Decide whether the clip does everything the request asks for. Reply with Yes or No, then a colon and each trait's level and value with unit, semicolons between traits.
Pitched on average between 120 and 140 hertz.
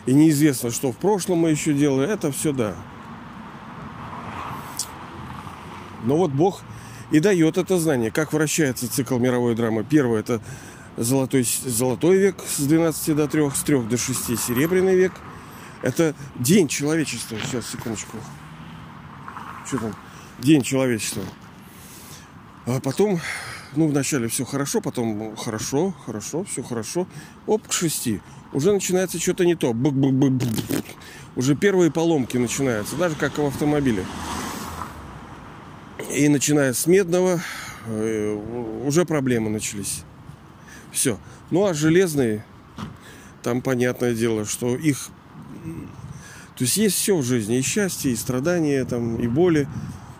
Yes: low, 135 Hz